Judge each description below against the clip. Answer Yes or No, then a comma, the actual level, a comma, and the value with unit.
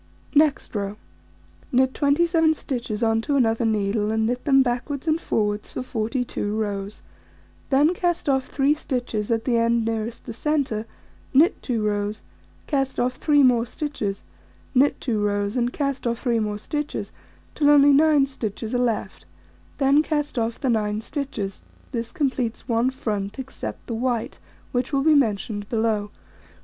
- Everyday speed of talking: Yes, average, 160 wpm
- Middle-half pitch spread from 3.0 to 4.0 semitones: No, average, 4.4 semitones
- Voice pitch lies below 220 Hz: No, high, 245 Hz